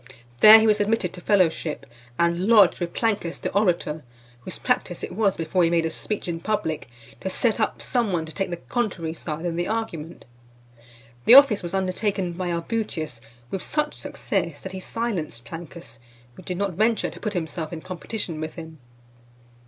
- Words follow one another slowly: No, average, 185 wpm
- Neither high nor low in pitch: Yes, medium, 180 Hz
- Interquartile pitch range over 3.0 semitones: Yes, average, 4.3 semitones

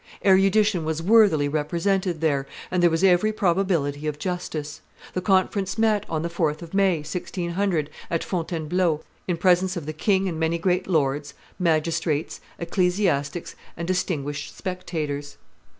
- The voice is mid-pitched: Yes, medium, 170 Hz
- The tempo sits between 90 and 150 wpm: Yes, average, 140 wpm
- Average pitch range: Yes, average, 3.3 semitones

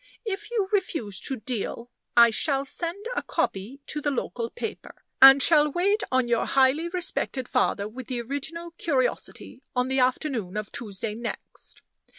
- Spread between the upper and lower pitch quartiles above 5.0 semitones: Yes, wide, 5.6 semitones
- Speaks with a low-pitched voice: No, very high, 265 Hz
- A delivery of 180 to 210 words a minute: No, average, 160 wpm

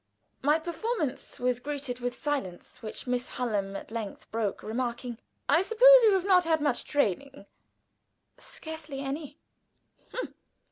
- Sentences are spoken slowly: Yes, slow, 130 wpm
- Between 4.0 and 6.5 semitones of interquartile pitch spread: Yes, average, 4.9 semitones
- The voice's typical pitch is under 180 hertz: No, very high, 275 Hz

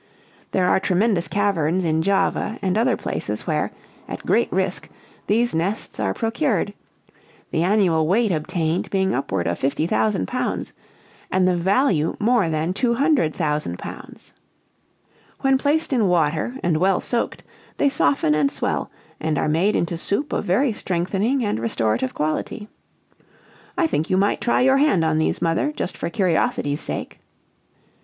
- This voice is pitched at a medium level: Yes, medium, 180 Hz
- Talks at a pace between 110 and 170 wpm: Yes, average, 150 wpm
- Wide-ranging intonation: Yes, wide, 5.7 semitones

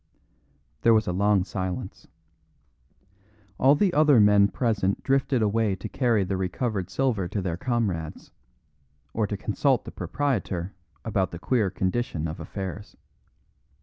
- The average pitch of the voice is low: Yes, low, 105 Hz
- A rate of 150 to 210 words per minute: No, slow, 135 wpm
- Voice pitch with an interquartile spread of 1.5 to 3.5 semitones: No, average, 4.3 semitones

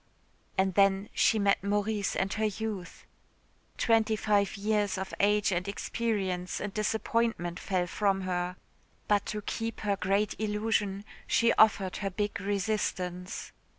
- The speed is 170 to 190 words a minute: No, slow, 135 wpm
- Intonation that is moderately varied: No, narrow, 1.9 semitones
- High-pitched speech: Yes, high, 200 Hz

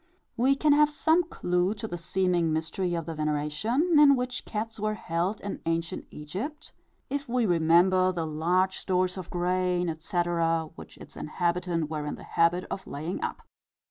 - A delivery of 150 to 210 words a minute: Yes, average, 170 wpm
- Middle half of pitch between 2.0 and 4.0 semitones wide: No, average, 4.7 semitones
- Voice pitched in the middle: Yes, medium, 180 Hz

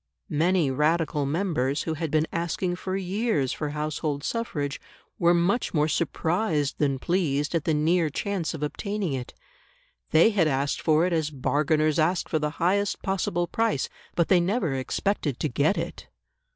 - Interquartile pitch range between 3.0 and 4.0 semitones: Yes, average, 3.6 semitones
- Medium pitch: Yes, medium, 160 Hz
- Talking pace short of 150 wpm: No, average, 165 wpm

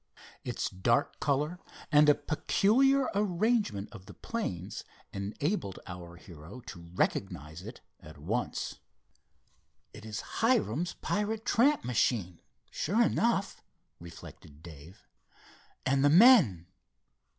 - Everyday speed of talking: No, slow, 105 wpm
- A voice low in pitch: Yes, low, 120 Hz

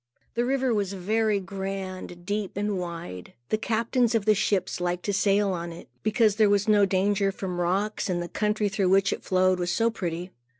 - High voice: Yes, high, 195 Hz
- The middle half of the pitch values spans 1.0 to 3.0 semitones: Yes, narrow, 2.6 semitones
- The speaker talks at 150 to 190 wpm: No, average, 200 wpm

